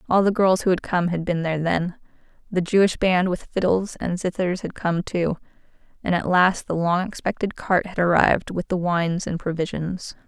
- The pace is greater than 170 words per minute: Yes, average, 200 wpm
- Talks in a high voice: No, medium, 180 Hz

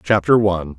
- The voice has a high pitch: No, very low, 95 Hz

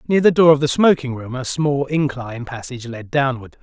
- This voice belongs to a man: Yes, male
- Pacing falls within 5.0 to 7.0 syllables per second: Yes, 5.5 syllables/s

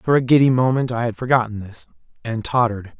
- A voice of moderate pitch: No, low, 120 Hz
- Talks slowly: No, average, 200 wpm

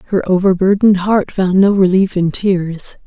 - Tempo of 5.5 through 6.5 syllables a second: No, 4.7 syllables/s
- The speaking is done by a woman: Yes, female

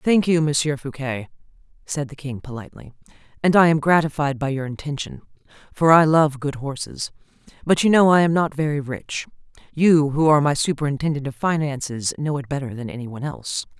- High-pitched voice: No, medium, 145 Hz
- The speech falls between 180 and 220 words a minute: Yes, average, 185 wpm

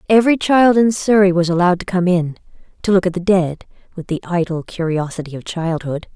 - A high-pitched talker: No, medium, 180 Hz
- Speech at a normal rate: Yes, average, 195 wpm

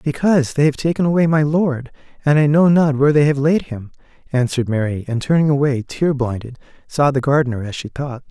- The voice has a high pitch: No, medium, 140 Hz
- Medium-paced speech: No, fast, 210 wpm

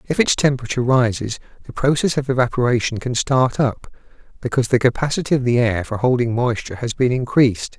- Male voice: Yes, male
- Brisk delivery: No, average, 175 wpm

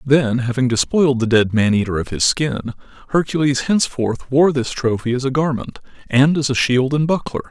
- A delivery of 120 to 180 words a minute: No, average, 190 wpm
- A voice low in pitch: Yes, low, 130 Hz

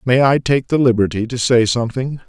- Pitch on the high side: No, low, 125 Hz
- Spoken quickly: Yes, fast, 210 wpm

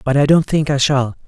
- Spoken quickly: Yes, fast, 285 wpm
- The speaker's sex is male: Yes, male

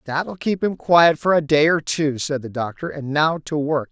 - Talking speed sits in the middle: No, fast, 260 wpm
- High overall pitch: No, medium, 150 Hz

